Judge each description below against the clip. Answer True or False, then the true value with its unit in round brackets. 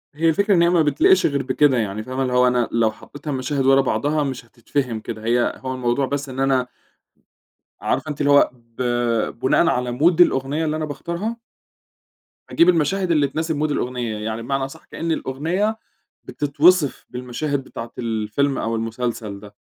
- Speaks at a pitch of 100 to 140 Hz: True (135 Hz)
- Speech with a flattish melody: False (4.1 semitones)